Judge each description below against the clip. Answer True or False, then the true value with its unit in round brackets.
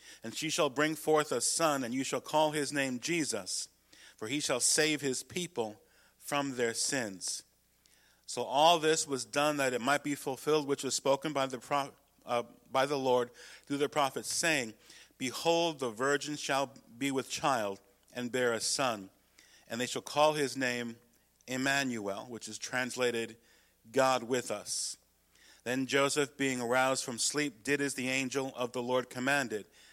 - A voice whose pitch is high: False (135 Hz)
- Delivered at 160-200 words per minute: True (170 wpm)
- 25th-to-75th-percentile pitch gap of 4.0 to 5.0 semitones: False (2.9 semitones)